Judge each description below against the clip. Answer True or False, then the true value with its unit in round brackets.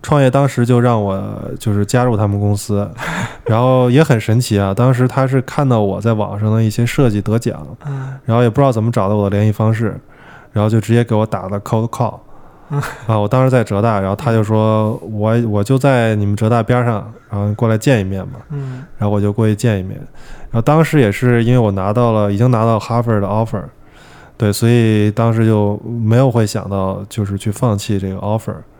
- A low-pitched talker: True (115 Hz)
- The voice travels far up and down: False (3.0 semitones)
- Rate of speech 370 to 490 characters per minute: False (330 characters per minute)